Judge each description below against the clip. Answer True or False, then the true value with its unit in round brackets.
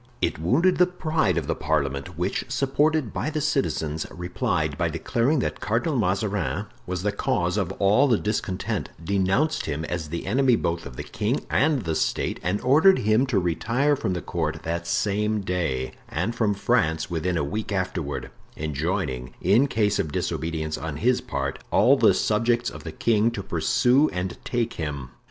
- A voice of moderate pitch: False (100 Hz)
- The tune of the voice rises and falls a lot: True (6.9 semitones)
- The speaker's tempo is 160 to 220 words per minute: True (175 wpm)